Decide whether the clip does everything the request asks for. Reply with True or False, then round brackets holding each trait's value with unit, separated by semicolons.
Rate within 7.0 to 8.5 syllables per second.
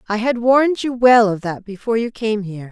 False (5.9 syllables/s)